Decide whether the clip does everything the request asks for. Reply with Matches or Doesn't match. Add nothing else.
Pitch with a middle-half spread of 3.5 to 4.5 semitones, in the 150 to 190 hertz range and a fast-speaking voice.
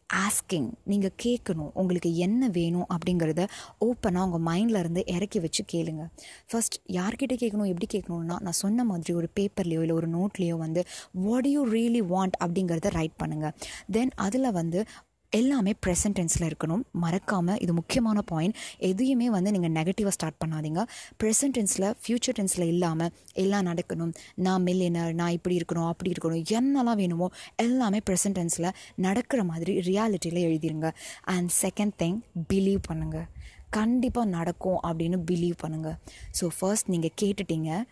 Matches